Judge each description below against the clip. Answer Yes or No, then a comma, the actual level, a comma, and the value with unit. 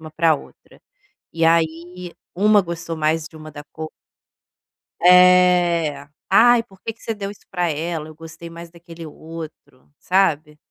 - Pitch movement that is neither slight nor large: No, narrow, 2.3 semitones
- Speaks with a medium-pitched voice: Yes, medium, 165 Hz